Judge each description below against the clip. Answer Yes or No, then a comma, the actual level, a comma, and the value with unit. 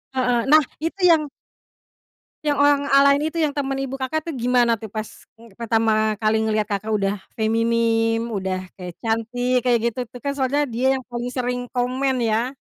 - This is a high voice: Yes, high, 245 Hz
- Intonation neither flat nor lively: Yes, average, 3.4 semitones